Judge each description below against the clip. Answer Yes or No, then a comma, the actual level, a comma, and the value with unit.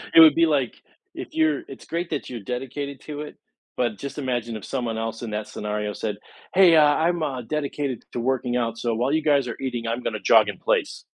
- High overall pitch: No, low, 130 Hz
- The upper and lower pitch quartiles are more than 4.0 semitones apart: Yes, average, 4.4 semitones